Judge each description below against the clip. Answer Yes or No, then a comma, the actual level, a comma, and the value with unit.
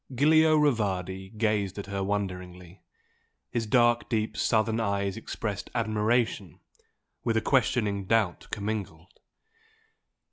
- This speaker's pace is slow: Yes, slow, 105 wpm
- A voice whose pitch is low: Yes, low, 105 Hz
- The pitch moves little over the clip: No, average, 3.0 semitones